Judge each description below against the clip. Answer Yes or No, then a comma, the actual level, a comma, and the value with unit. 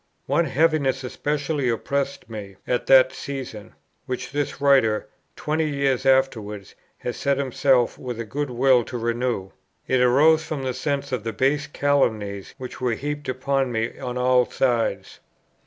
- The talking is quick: No, average, 155 wpm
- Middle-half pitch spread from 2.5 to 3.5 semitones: Yes, average, 2.9 semitones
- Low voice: Yes, low, 130 Hz